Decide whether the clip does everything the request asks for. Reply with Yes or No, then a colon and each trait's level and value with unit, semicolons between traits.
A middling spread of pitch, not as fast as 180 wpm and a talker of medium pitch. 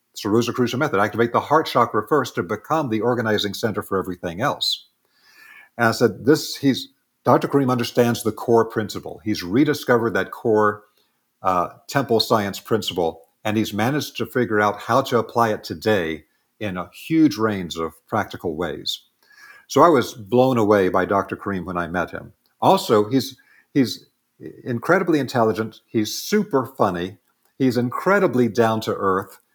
No: average, 3.8 semitones; average, 155 wpm; low, 115 Hz